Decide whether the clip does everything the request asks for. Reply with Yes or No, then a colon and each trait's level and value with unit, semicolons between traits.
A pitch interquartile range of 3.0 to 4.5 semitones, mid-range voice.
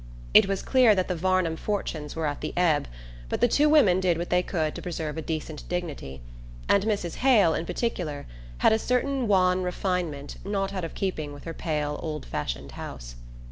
Yes: average, 4.2 semitones; medium, 175 Hz